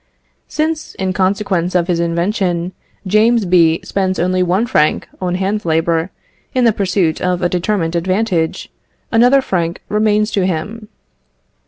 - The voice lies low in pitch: No, medium, 185 Hz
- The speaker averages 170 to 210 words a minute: No, average, 140 wpm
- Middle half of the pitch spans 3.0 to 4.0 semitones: Yes, average, 3.6 semitones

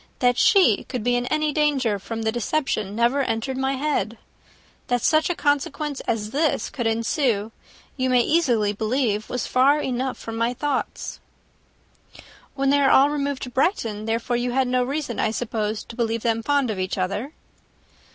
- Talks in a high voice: Yes, very high, 250 Hz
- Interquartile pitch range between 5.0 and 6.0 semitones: No, average, 3.9 semitones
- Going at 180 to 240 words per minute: No, average, 170 wpm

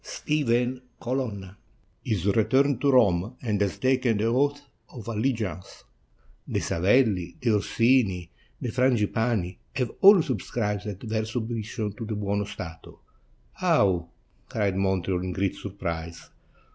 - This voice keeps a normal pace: No, slow, 130 wpm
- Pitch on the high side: No, low, 110 Hz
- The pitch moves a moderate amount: Yes, average, 4.3 semitones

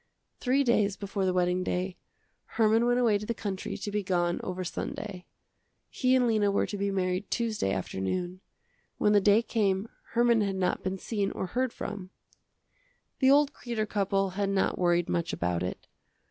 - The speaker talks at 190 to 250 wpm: No, average, 175 wpm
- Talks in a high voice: Yes, high, 200 Hz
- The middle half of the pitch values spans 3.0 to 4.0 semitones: Yes, average, 3.4 semitones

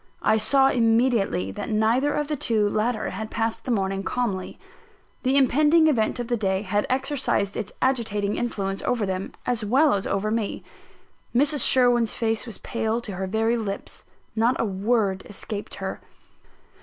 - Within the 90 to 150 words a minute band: No, average, 165 wpm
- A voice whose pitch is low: No, high, 225 Hz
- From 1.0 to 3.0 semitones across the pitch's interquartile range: No, average, 3.4 semitones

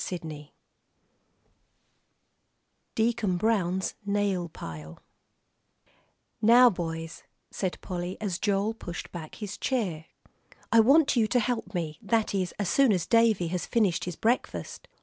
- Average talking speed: No, slow, 125 wpm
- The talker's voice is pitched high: Yes, high, 195 Hz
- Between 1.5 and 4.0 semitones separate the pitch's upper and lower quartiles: No, average, 4.5 semitones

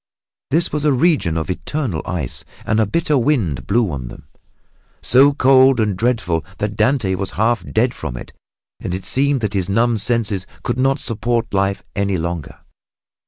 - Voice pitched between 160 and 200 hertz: No, low, 110 Hz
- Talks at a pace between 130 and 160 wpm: No, average, 170 wpm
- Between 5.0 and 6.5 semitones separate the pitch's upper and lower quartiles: Yes, wide, 5.6 semitones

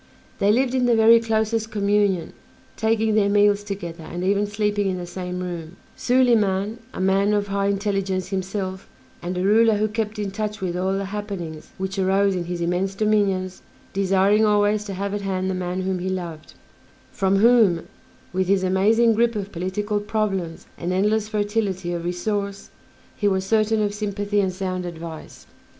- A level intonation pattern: Yes, narrow, 2.1 semitones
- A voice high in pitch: Yes, high, 200 Hz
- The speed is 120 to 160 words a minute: No, average, 175 wpm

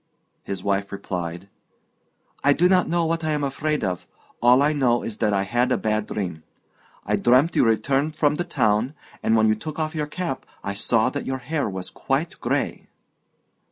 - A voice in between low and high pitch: No, low, 125 Hz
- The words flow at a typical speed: Yes, average, 190 wpm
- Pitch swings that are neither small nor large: No, wide, 6.3 semitones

